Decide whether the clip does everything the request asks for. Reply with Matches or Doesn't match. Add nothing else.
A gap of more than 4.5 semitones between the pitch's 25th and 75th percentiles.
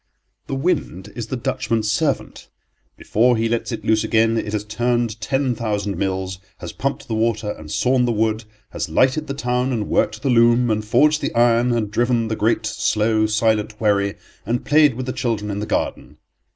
Doesn't match